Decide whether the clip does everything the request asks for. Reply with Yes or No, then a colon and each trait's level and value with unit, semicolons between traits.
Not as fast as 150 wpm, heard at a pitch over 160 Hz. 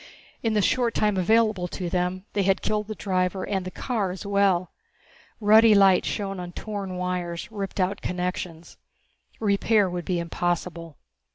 No: average, 160 wpm; high, 190 Hz